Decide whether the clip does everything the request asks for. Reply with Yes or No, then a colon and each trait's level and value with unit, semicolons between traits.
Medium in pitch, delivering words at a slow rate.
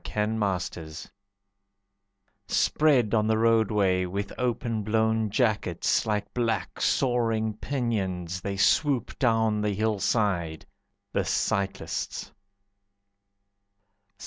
No: low, 110 Hz; slow, 90 wpm